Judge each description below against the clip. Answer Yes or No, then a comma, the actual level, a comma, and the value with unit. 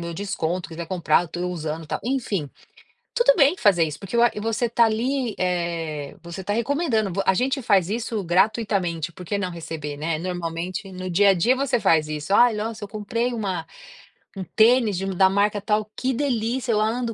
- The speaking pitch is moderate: No, high, 200 Hz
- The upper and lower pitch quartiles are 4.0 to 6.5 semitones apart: Yes, average, 5.1 semitones